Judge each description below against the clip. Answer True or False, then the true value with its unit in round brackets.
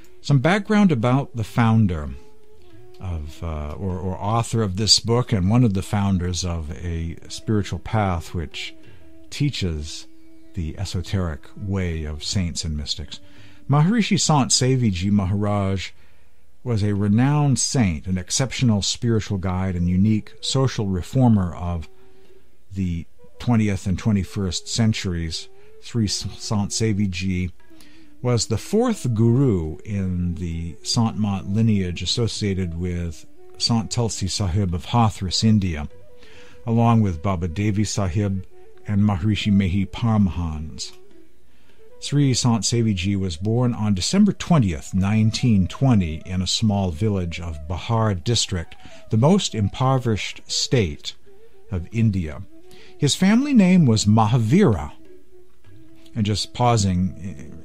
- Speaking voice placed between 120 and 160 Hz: False (105 Hz)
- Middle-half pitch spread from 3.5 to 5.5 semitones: True (4.7 semitones)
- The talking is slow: True (115 wpm)